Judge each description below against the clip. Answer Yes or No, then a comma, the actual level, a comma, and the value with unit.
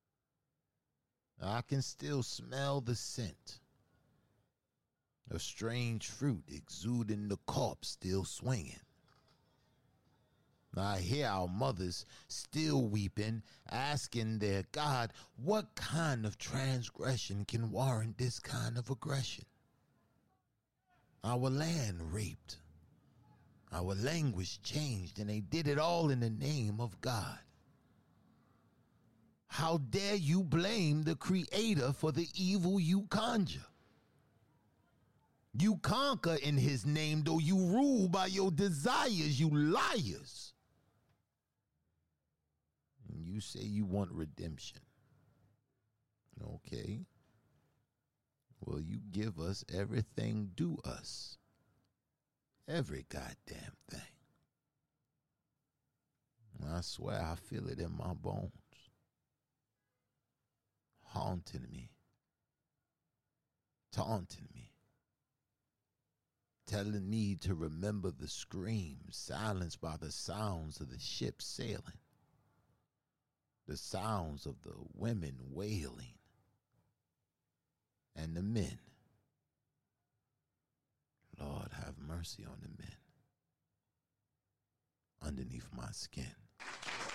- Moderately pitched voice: No, low, 120 Hz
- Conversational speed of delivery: No, slow, 95 wpm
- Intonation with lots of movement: Yes, wide, 6.5 semitones